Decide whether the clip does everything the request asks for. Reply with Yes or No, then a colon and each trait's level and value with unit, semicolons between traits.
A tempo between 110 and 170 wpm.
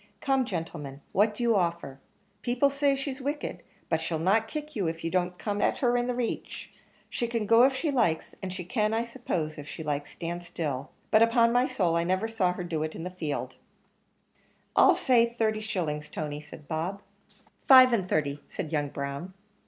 No: average, 200 wpm